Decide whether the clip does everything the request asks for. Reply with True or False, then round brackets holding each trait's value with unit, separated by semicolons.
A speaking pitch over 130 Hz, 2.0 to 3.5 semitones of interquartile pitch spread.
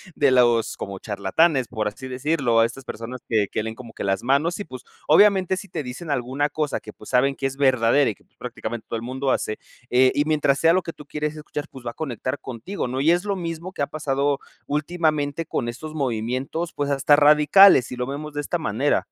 False (140 Hz; 3.9 semitones)